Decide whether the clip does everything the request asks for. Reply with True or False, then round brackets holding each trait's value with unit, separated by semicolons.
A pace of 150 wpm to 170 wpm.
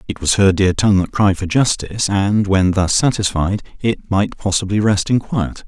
False (200 wpm)